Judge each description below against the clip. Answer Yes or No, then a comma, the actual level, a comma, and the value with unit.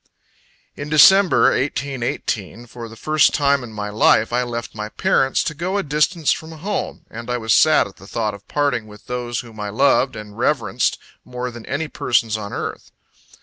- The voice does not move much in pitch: No, average, 4.7 semitones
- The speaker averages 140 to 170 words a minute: No, average, 190 wpm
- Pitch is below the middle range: Yes, low, 125 Hz